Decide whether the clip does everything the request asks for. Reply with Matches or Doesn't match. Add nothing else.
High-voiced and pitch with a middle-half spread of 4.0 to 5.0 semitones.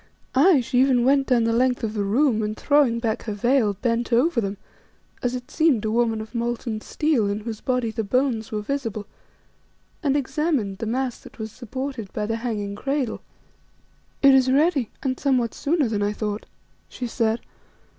Doesn't match